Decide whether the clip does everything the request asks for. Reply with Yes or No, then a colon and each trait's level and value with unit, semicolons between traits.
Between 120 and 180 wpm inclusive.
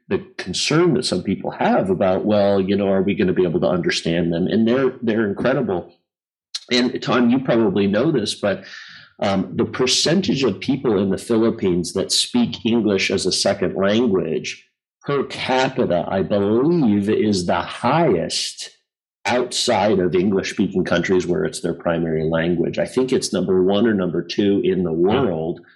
Yes: average, 170 wpm